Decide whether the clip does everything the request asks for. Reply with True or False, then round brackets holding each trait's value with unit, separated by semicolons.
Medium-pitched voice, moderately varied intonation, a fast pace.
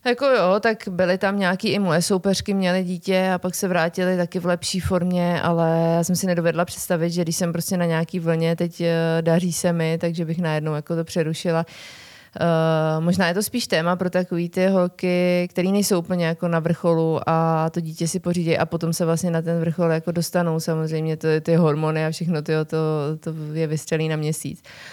False (170 Hz; 1.8 semitones; 205 wpm)